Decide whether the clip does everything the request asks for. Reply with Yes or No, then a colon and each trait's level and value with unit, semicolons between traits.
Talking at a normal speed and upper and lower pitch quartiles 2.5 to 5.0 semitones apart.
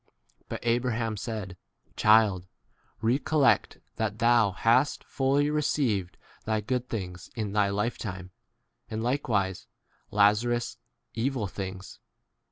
No: slow, 110 wpm; average, 3.4 semitones